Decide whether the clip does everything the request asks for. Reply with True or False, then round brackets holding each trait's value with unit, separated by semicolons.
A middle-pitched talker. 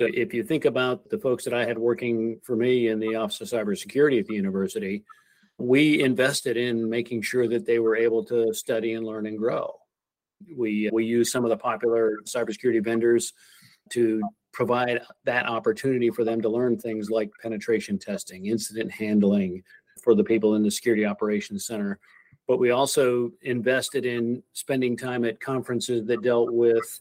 False (115 Hz)